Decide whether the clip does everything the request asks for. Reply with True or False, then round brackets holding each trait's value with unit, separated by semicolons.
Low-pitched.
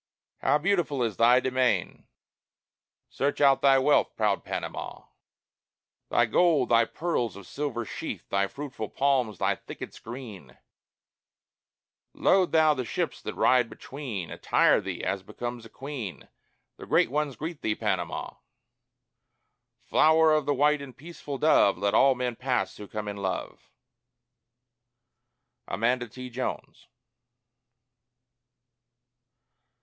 True (125 Hz)